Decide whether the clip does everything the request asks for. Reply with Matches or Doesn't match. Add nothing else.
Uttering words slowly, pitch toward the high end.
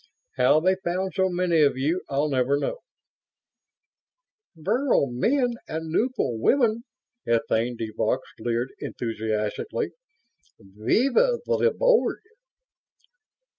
Doesn't match